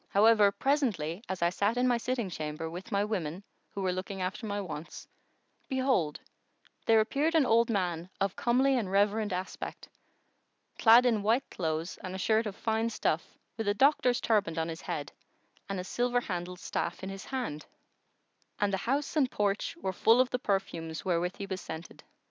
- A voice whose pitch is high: Yes, high, 200 Hz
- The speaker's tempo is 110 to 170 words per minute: No, average, 185 wpm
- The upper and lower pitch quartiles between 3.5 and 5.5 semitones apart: Yes, average, 4.5 semitones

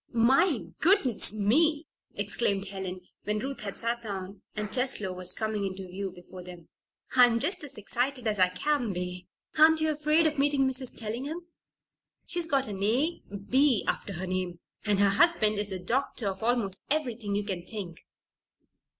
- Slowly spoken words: No, average, 165 wpm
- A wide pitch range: Yes, wide, 6.1 semitones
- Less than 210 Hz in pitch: No, high, 215 Hz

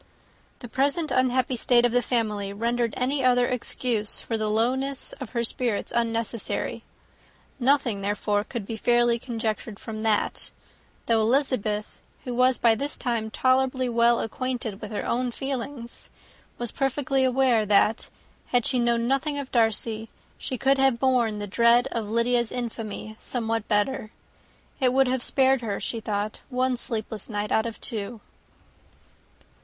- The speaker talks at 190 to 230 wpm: No, average, 150 wpm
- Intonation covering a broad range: No, narrow, 2.6 semitones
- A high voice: Yes, high, 235 Hz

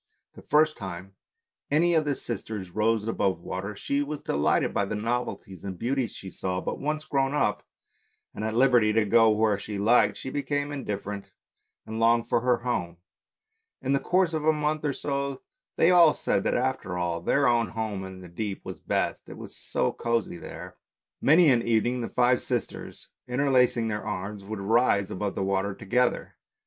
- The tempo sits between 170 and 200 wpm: Yes, average, 185 wpm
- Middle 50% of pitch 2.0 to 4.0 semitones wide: No, average, 5.3 semitones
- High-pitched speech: No, low, 115 Hz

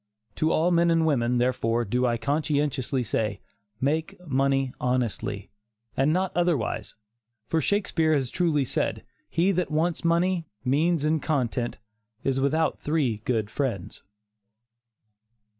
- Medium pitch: Yes, medium, 145 Hz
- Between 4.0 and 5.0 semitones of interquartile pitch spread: Yes, average, 4.6 semitones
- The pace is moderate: No, slow, 125 wpm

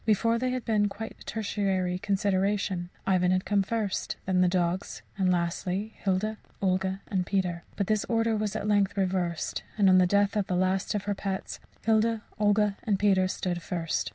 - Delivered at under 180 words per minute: No, average, 185 wpm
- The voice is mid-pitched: No, high, 195 Hz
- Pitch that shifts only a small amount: Yes, narrow, 2.1 semitones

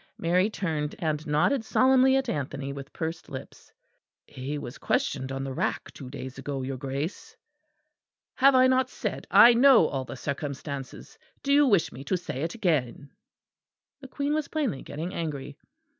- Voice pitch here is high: No, medium, 155 Hz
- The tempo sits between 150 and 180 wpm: Yes, average, 165 wpm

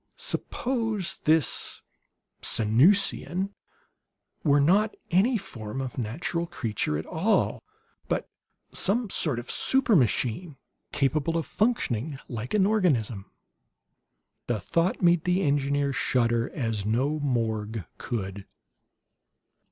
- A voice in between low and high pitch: Yes, medium, 145 Hz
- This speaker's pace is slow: Yes, slow, 100 wpm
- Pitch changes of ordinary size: No, wide, 7.8 semitones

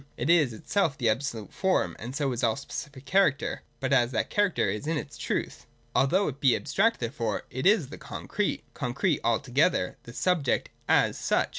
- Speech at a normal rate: Yes, average, 185 wpm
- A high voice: No, medium, 140 Hz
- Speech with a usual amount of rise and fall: No, wide, 6.2 semitones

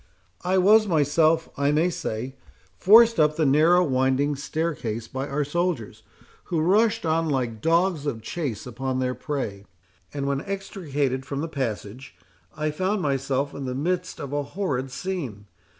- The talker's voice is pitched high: No, medium, 145 Hz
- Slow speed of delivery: No, average, 155 wpm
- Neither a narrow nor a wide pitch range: Yes, average, 4.7 semitones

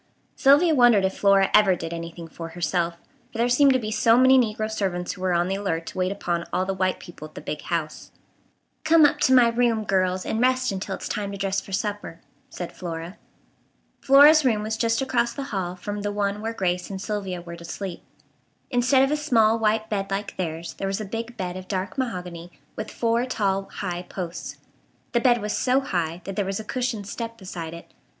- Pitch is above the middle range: Yes, high, 200 Hz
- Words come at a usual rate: No, fast, 215 wpm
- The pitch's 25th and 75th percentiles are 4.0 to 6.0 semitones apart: Yes, average, 4.4 semitones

